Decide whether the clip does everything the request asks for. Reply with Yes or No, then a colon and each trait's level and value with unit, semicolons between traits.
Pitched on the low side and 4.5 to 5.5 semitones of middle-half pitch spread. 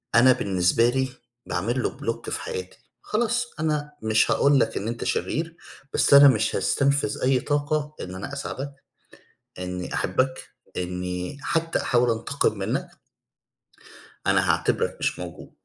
Yes: low, 130 Hz; average, 5.0 semitones